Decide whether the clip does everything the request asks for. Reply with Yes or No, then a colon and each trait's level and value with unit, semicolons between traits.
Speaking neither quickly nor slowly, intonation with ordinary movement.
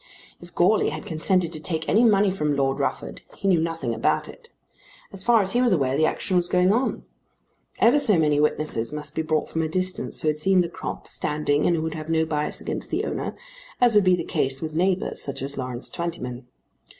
No: fast, 220 wpm; average, 3.7 semitones